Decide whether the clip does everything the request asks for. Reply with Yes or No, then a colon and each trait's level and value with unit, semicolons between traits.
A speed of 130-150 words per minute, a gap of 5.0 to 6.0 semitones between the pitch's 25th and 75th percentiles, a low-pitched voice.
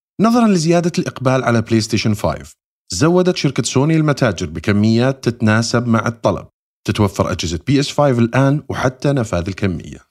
Yes: fast, 135 wpm; wide, 5.5 semitones; low, 120 Hz